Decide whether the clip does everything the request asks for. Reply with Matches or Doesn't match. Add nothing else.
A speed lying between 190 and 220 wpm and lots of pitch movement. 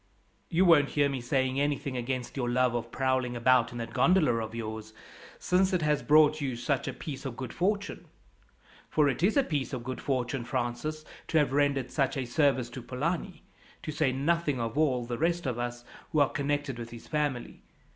Doesn't match